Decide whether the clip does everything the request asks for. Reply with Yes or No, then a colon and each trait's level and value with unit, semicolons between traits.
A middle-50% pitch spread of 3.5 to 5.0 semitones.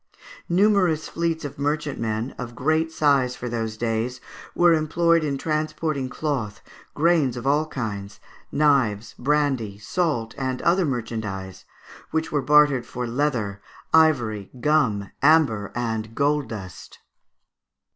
No: wide, 5.5 semitones